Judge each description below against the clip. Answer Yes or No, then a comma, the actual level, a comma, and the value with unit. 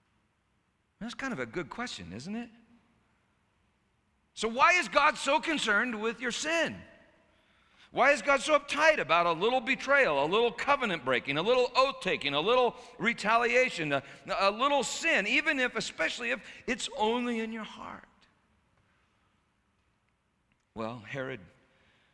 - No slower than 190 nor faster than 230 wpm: No, average, 140 wpm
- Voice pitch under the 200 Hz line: No, high, 230 Hz